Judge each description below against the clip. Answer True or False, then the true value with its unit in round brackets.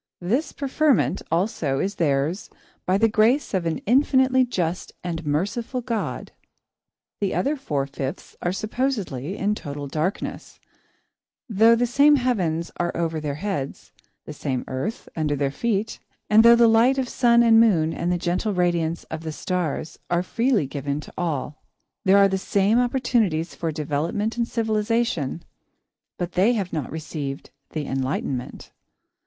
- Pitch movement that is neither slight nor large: False (6.7 semitones)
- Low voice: False (185 Hz)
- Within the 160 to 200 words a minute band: False (150 wpm)